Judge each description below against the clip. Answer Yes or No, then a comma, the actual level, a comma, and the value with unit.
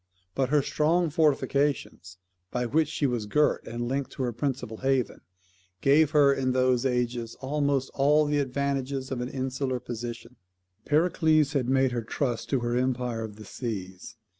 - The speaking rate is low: No, average, 165 wpm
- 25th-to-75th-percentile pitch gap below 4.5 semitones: Yes, average, 2.8 semitones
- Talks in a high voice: No, low, 130 Hz